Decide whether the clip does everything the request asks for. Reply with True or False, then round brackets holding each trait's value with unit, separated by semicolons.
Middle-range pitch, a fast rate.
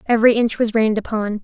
False (220 Hz; 210 wpm)